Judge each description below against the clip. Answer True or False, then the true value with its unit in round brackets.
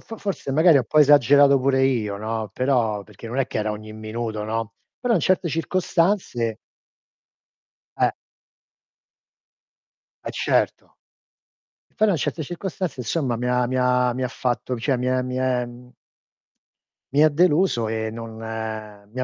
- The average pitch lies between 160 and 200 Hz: False (125 Hz)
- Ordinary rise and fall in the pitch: True (4.4 semitones)